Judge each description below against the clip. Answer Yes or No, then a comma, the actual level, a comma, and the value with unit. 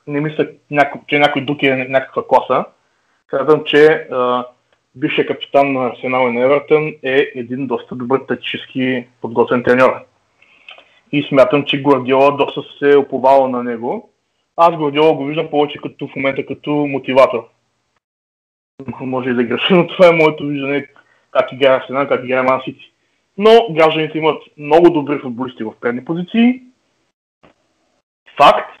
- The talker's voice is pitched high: No, medium, 140 Hz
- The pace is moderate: Yes, average, 140 wpm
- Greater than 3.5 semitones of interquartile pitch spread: No, average, 2.8 semitones